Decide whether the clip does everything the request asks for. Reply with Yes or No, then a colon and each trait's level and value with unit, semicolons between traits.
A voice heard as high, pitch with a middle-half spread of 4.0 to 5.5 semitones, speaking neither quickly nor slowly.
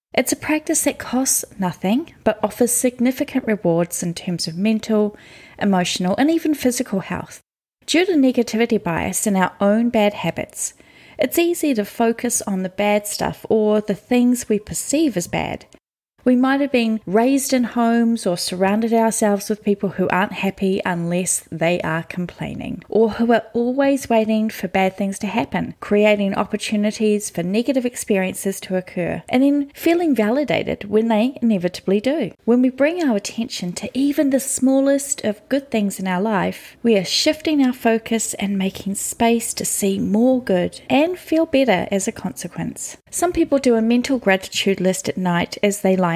Yes: high, 220 Hz; average, 4.7 semitones; average, 170 wpm